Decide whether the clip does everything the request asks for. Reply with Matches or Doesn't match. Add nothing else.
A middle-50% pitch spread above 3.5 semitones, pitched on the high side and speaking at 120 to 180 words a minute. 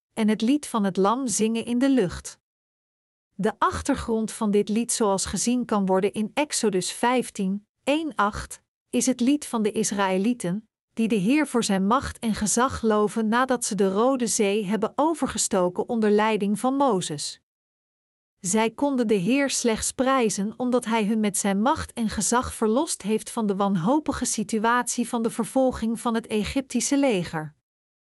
Doesn't match